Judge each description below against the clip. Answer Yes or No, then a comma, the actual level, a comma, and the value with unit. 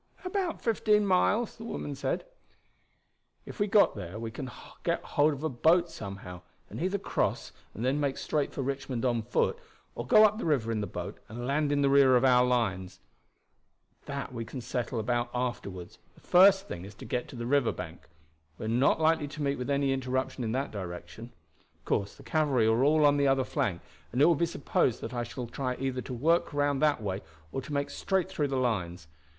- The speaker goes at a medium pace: No, fast, 215 wpm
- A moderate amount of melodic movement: Yes, average, 4.4 semitones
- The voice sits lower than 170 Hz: Yes, low, 135 Hz